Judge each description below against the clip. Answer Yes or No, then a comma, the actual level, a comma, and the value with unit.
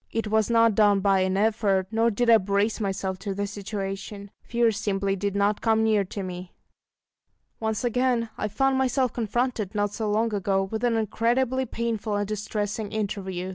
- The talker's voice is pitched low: No, high, 210 Hz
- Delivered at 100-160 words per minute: No, average, 175 wpm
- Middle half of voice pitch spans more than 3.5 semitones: No, narrow, 2.4 semitones